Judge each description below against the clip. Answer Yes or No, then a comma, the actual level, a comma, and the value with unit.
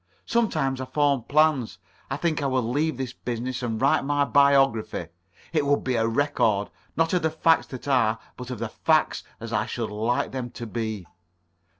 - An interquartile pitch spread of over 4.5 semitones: No, average, 3.8 semitones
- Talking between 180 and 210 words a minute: Yes, average, 190 wpm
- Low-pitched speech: Yes, low, 130 Hz